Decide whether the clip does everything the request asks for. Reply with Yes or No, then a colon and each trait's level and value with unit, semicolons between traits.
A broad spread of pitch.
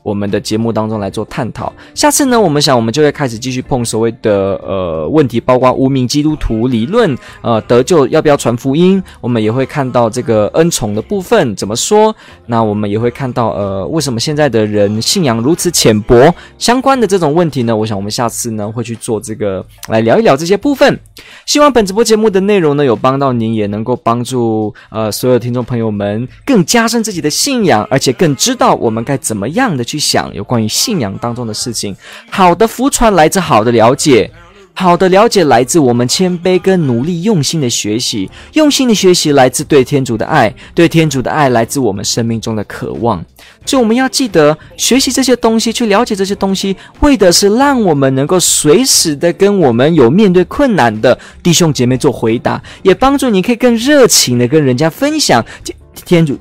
Yes: wide, 9.0 semitones